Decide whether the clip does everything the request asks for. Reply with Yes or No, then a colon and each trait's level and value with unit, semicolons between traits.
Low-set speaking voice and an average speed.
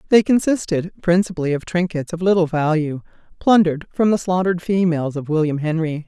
No: medium, 170 Hz; average, 160 wpm